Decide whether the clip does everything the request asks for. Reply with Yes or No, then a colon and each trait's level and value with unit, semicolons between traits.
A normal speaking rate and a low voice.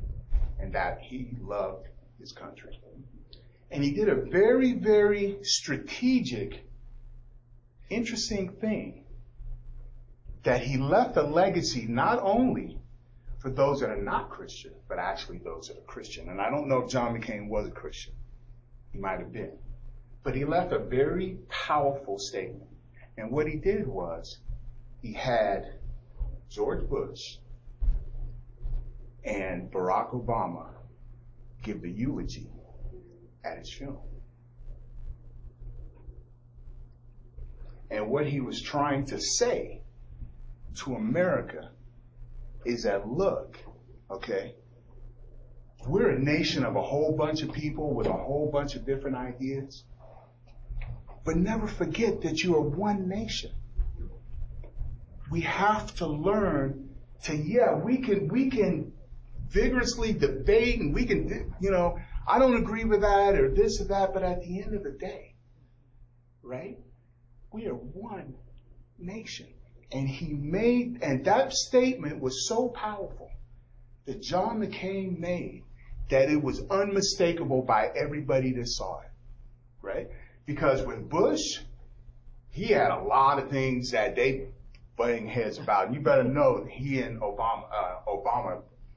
No: slow, 130 wpm; low, 125 Hz